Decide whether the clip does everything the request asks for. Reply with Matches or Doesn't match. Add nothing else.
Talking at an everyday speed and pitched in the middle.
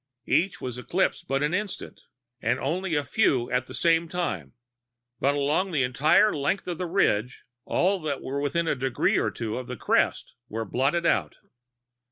Matches